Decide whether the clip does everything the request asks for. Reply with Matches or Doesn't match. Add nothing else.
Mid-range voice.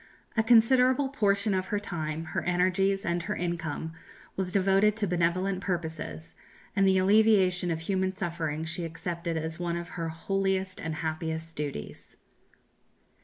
Matches